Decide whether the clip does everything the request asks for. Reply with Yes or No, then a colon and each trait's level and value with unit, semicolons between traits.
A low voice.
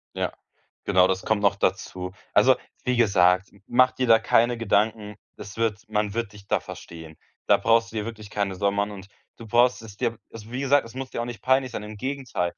Yes: low, 110 Hz